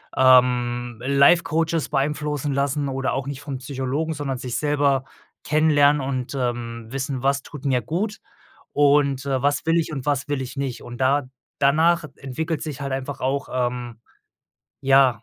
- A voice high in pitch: No, medium, 140 Hz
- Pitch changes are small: Yes, narrow, 2.2 semitones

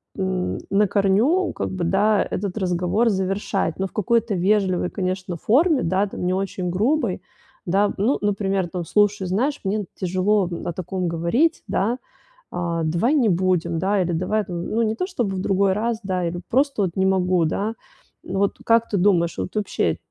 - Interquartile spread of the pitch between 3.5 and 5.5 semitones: No, average, 2.8 semitones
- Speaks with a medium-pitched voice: No, high, 195 Hz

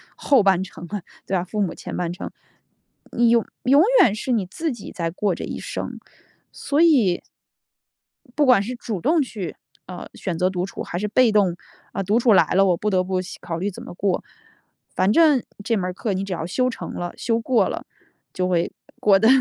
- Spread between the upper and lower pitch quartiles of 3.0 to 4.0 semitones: No, average, 4.6 semitones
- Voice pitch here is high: Yes, high, 200 Hz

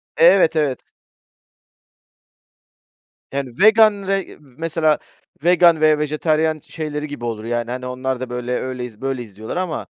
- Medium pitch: Yes, medium, 150 Hz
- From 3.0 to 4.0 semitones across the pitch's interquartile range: No, average, 4.5 semitones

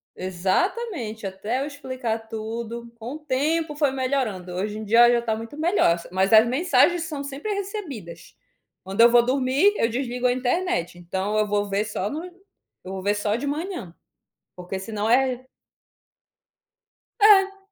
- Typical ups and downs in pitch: No, wide, 6.1 semitones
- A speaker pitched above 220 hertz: Yes, high, 240 Hz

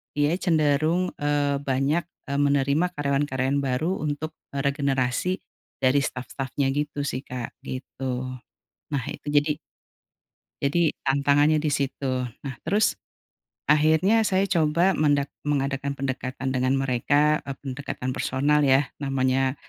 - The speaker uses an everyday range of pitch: No, narrow, 2.0 semitones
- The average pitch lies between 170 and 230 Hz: No, medium, 140 Hz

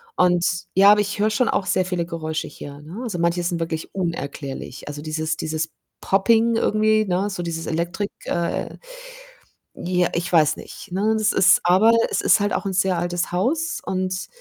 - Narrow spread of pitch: No, average, 3.4 semitones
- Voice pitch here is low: No, medium, 180 Hz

